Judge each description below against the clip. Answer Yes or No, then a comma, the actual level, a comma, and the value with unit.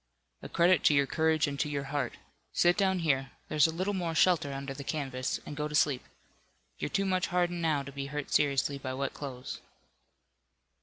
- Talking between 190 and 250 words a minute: Yes, average, 200 wpm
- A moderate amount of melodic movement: Yes, average, 3.6 semitones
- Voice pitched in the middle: Yes, medium, 150 Hz